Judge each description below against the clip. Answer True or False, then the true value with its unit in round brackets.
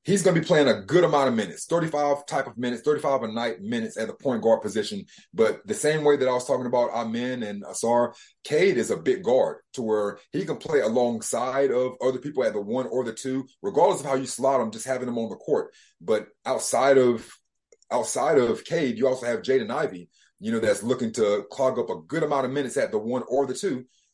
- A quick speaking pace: True (240 wpm)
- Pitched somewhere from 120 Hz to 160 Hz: True (135 Hz)